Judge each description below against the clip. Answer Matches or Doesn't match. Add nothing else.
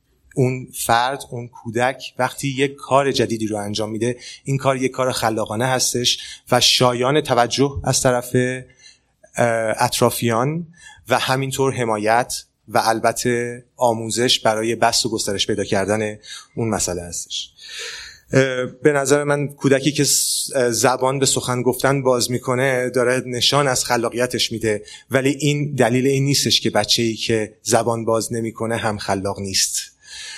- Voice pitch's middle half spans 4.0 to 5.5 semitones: Doesn't match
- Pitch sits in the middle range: Doesn't match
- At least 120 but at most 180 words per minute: Matches